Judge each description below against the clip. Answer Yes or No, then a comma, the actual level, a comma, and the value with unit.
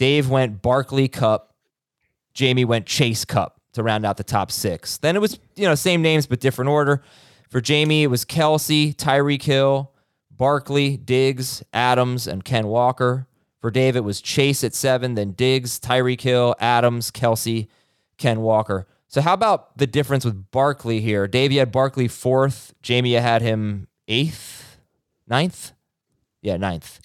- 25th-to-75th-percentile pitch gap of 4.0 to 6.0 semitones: No, average, 3.4 semitones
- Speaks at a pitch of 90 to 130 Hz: Yes, low, 125 Hz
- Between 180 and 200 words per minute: No, average, 160 wpm